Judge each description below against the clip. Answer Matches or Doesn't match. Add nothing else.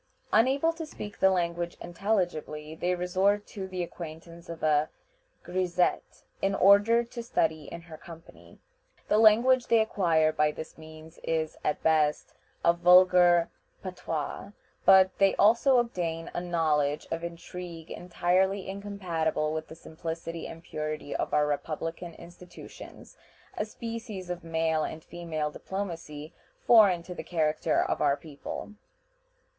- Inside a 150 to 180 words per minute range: Doesn't match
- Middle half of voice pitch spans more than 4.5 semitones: Doesn't match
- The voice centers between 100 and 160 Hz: Doesn't match